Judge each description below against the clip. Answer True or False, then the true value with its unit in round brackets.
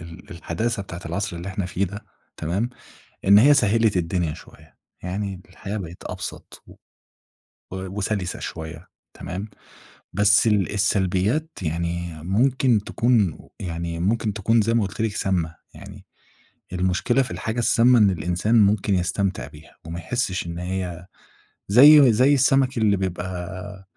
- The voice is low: True (95 Hz)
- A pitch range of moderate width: True (3.9 semitones)